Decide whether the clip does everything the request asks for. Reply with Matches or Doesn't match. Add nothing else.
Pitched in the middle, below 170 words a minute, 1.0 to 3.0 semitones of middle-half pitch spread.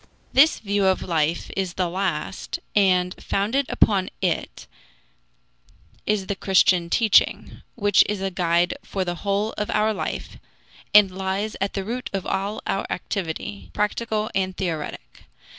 Doesn't match